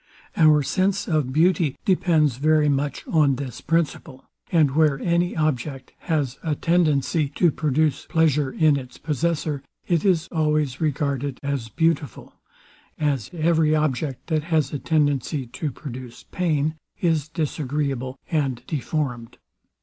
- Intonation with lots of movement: No, average, 2.8 semitones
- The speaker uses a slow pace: Yes, slow, 125 wpm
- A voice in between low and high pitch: Yes, medium, 150 Hz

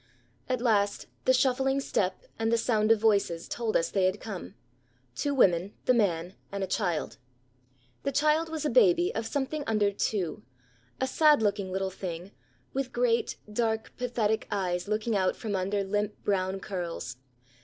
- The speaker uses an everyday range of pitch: Yes, average, 4.6 semitones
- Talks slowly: No, average, 165 wpm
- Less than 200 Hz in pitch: No, high, 210 Hz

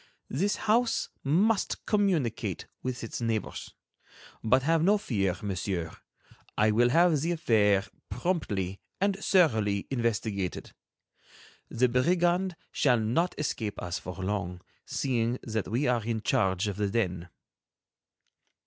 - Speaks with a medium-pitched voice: No, low, 115 Hz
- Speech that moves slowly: Yes, slow, 120 wpm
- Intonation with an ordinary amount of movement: No, wide, 8.4 semitones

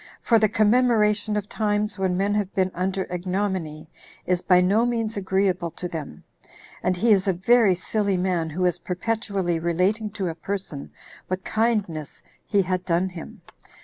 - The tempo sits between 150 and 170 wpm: Yes, average, 165 wpm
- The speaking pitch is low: No, high, 190 Hz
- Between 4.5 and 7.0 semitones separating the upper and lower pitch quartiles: No, average, 2.8 semitones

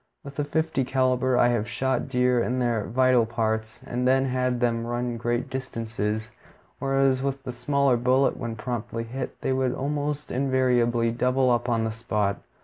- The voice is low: Yes, low, 125 Hz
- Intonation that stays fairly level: Yes, narrow, 2.1 semitones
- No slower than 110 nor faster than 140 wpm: No, average, 170 wpm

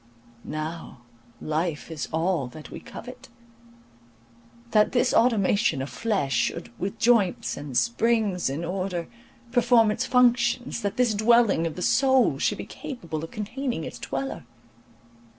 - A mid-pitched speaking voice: No, high, 200 Hz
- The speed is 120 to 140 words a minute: Yes, slow, 135 wpm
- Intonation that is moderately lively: No, wide, 6.6 semitones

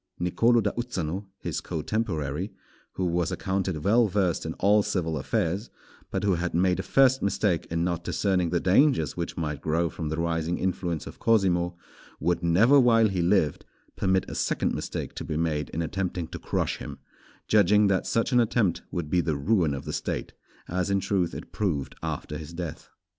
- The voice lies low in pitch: Yes, very low, 90 Hz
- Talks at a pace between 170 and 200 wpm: Yes, average, 185 wpm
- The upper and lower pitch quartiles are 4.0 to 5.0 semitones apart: No, average, 3.5 semitones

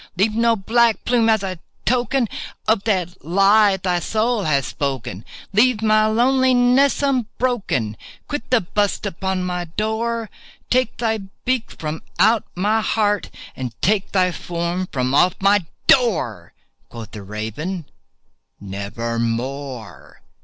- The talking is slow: Yes, slow, 125 wpm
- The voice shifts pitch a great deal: Yes, wide, 7.3 semitones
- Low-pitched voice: No, high, 195 Hz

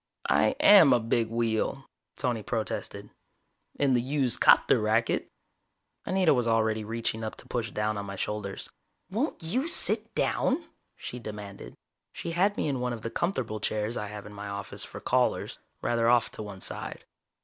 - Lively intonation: No, average, 3.9 semitones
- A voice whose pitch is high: No, low, 115 Hz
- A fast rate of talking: No, average, 170 wpm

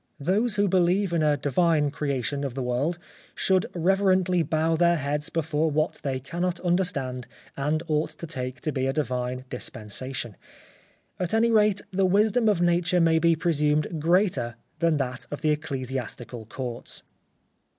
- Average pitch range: Yes, average, 4.8 semitones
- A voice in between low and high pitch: Yes, medium, 155 Hz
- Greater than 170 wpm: No, average, 155 wpm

